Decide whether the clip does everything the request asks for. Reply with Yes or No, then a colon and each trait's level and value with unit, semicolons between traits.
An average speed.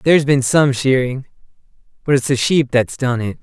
Yes: average, 195 wpm